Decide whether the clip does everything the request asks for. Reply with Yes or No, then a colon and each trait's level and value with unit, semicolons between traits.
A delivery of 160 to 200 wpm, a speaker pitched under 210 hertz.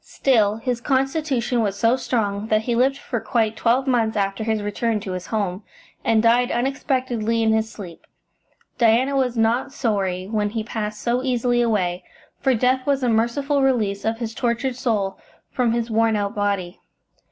No: average, 175 wpm; high, 230 Hz